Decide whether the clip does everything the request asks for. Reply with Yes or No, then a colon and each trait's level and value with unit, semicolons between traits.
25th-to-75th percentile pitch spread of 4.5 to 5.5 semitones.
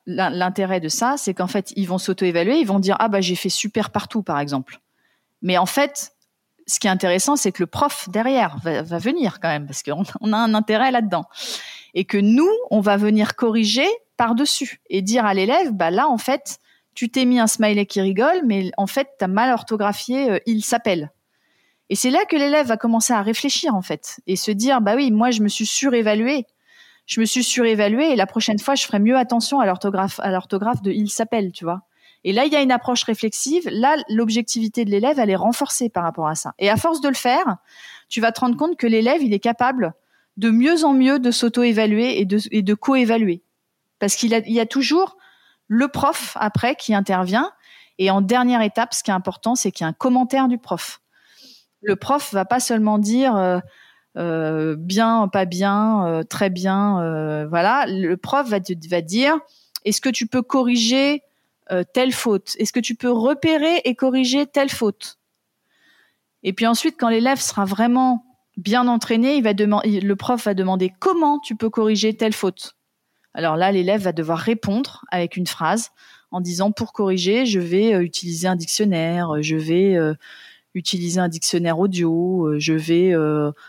Yes: average, 4.9 semitones